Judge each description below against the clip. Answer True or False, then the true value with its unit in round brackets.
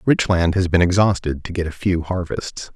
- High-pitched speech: False (90 Hz)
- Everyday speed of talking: False (220 wpm)